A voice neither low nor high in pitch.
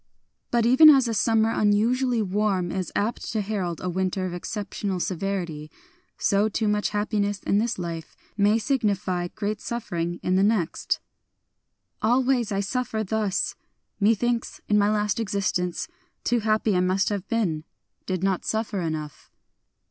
No: high, 205 Hz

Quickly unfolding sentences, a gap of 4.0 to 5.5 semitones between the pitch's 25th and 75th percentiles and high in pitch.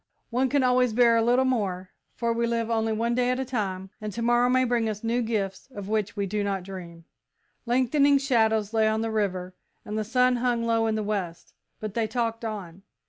No: fast, 220 wpm; average, 2.9 semitones; high, 225 Hz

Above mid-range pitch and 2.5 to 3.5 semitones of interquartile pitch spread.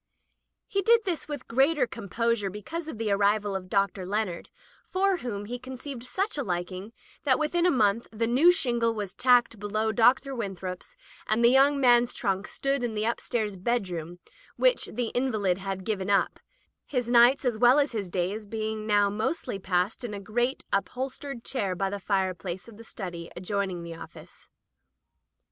No: high, 220 Hz; average, 4.4 semitones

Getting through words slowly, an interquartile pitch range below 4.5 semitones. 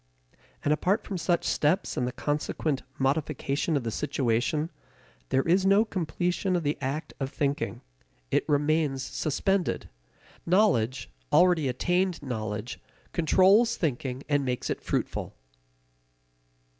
No: slow, 120 wpm; average, 4.9 semitones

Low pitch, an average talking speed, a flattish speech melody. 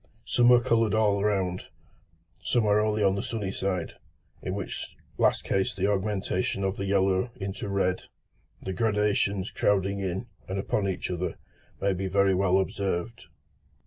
Yes: low, 100 Hz; average, 150 wpm; narrow, 1.6 semitones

